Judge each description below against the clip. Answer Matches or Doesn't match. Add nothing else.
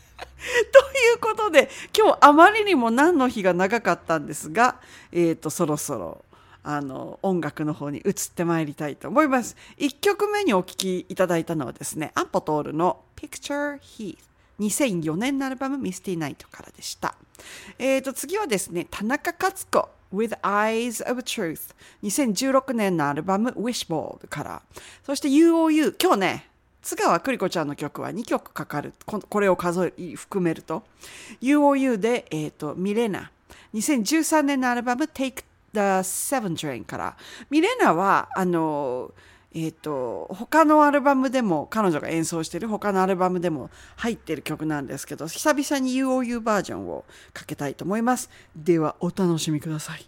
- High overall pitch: Matches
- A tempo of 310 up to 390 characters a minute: Matches